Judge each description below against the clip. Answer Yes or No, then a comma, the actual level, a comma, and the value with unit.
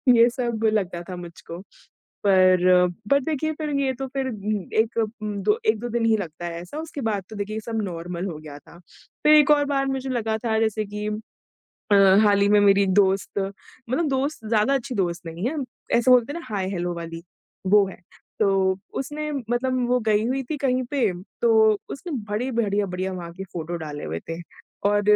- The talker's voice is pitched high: Yes, high, 215 Hz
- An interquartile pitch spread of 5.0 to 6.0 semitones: Yes, average, 5.3 semitones